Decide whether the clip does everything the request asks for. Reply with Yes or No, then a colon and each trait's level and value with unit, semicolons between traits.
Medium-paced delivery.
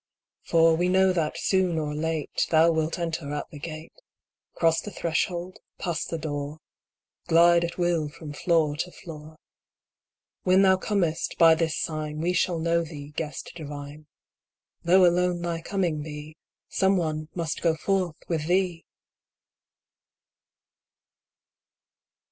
No: slow, 130 wpm